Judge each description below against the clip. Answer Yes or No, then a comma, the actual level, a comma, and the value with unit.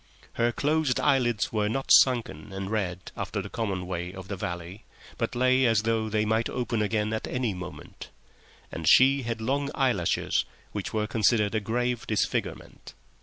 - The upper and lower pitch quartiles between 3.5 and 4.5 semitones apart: Yes, average, 3.9 semitones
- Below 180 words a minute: Yes, average, 170 wpm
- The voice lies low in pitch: Yes, low, 110 Hz